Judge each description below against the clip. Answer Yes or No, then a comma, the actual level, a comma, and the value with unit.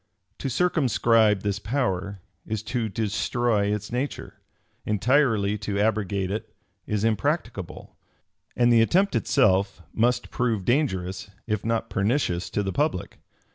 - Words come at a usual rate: No, slow, 125 wpm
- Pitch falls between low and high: No, low, 110 Hz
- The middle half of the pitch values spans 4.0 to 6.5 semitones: No, average, 3.5 semitones